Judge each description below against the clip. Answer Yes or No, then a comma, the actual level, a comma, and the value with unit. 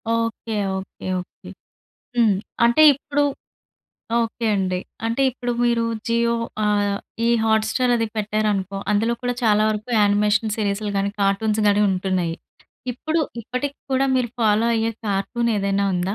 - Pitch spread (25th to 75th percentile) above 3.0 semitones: No, average, 2.7 semitones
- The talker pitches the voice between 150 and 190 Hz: No, high, 215 Hz